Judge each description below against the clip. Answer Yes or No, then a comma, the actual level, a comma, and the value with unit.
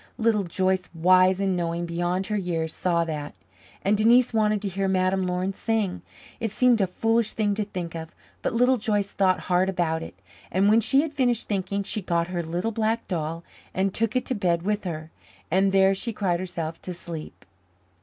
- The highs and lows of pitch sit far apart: No, average, 3.5 semitones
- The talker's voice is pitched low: No, high, 190 Hz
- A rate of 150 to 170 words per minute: No, average, 195 wpm